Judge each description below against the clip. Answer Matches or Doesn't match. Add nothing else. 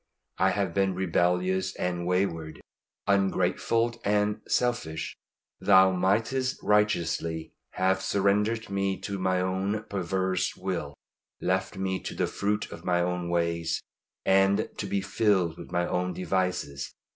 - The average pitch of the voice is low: Matches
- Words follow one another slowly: Matches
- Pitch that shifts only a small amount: Matches